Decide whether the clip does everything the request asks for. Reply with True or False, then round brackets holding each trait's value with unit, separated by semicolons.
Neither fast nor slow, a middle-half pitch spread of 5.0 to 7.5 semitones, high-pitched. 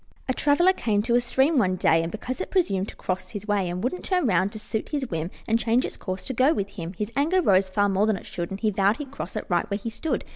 False (285 wpm; 5.5 semitones; 215 Hz)